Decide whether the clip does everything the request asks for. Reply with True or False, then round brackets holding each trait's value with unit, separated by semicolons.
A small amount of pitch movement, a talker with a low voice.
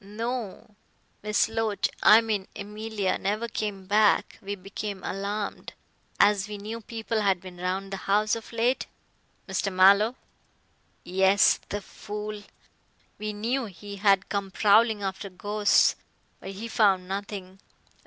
False (1.7 semitones; 205 Hz)